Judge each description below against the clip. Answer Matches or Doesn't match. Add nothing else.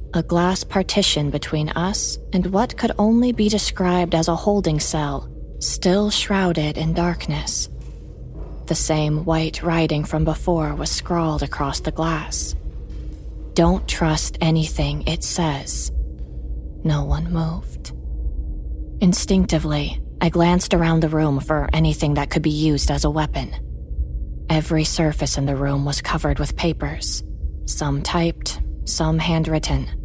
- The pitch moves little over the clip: Doesn't match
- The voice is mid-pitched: Matches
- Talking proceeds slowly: Matches